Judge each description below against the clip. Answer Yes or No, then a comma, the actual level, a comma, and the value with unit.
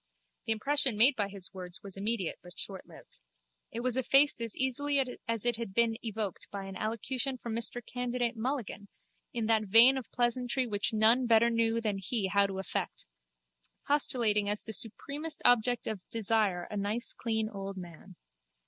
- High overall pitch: Yes, high, 225 Hz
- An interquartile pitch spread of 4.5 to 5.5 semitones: No, average, 3.4 semitones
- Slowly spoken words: No, average, 170 wpm